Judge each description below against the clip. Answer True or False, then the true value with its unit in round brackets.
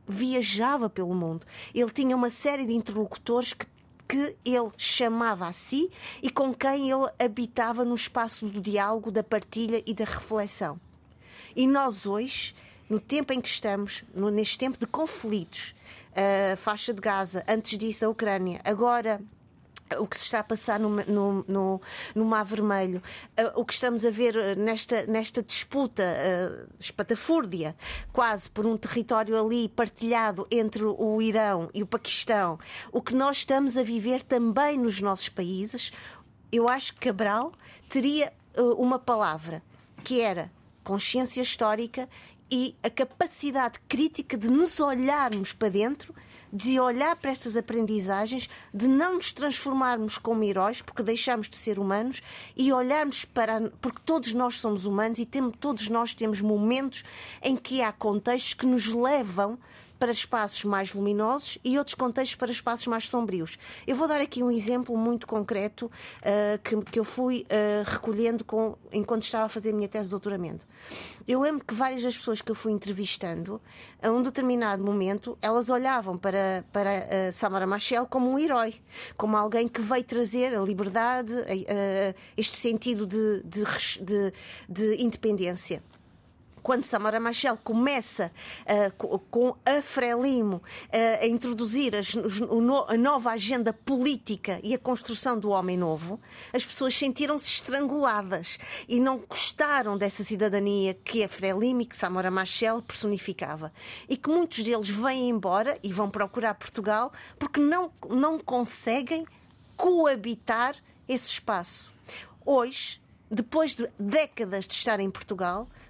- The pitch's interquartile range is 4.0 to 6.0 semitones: False (3.5 semitones)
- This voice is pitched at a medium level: False (230 Hz)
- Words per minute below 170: True (150 wpm)